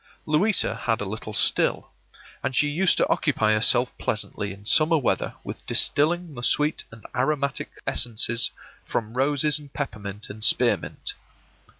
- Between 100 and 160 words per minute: Yes, average, 140 wpm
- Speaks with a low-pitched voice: Yes, low, 125 Hz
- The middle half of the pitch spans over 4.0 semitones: Yes, wide, 5.5 semitones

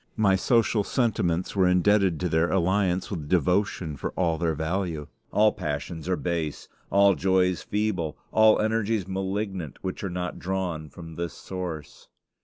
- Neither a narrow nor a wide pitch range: Yes, average, 3.2 semitones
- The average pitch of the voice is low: Yes, very low, 90 Hz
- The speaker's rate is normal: Yes, average, 150 wpm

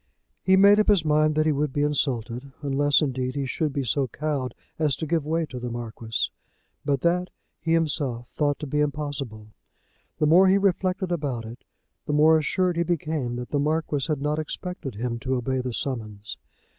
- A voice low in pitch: No, medium, 145 Hz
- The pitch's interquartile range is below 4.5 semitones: Yes, average, 3.8 semitones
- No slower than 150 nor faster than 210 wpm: Yes, average, 195 wpm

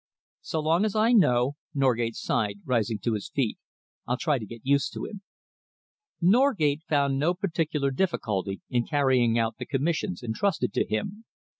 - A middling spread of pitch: No, wide, 6.3 semitones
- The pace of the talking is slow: No, average, 160 wpm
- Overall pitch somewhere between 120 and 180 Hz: Yes, medium, 140 Hz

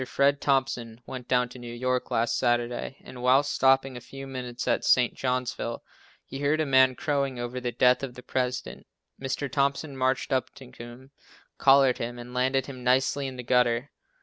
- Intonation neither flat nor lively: No, narrow, 1.7 semitones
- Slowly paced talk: No, average, 185 wpm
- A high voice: No, low, 130 Hz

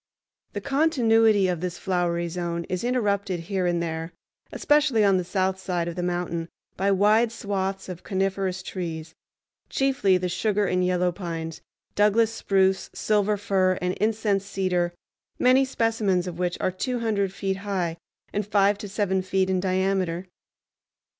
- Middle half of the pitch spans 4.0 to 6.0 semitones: No, narrow, 2.5 semitones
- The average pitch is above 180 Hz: Yes, high, 190 Hz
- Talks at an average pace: Yes, average, 155 wpm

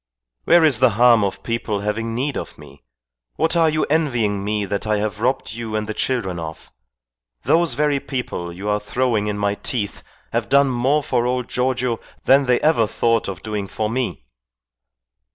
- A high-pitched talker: No, low, 115 Hz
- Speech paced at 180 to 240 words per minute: Yes, average, 185 wpm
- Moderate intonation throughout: Yes, average, 3.9 semitones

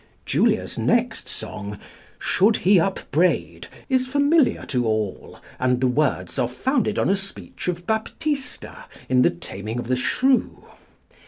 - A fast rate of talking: No, average, 140 wpm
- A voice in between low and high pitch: Yes, medium, 175 Hz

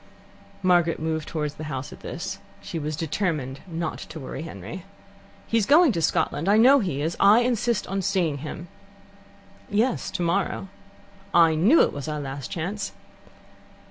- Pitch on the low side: No, medium, 170 Hz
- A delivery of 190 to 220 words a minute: No, average, 155 wpm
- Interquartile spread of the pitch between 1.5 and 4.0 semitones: No, average, 4.7 semitones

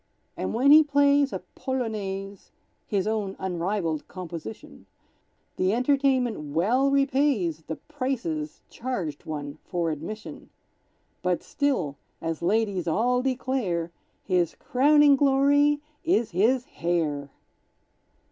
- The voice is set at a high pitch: Yes, high, 215 Hz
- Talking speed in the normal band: No, slow, 105 wpm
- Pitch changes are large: Yes, wide, 7.9 semitones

